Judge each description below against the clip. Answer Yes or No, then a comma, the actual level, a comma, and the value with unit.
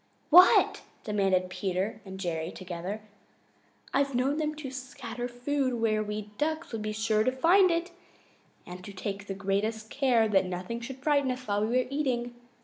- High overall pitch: Yes, high, 225 Hz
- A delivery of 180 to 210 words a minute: No, average, 170 wpm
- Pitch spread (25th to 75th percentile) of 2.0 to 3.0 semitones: No, average, 5.1 semitones